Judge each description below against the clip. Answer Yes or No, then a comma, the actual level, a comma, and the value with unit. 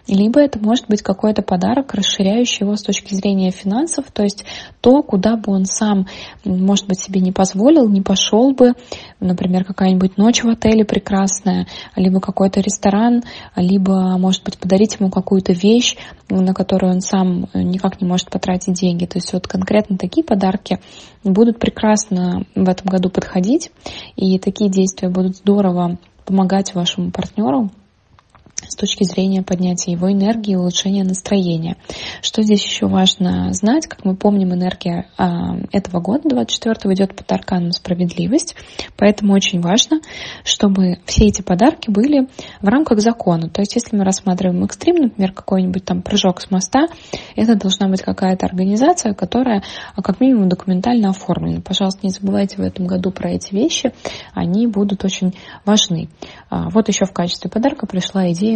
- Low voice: No, high, 195 Hz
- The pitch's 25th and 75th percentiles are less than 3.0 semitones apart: Yes, narrow, 2.4 semitones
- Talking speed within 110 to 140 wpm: No, average, 155 wpm